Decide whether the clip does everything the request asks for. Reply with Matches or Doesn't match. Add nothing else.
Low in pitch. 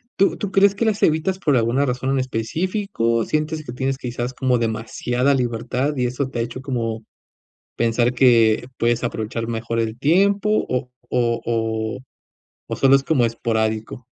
Matches